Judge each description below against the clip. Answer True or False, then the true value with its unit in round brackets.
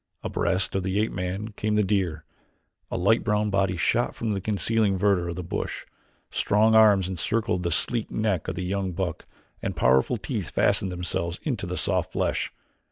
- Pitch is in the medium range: False (95 Hz)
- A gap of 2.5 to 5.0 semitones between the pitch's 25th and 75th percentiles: True (2.9 semitones)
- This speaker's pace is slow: False (180 wpm)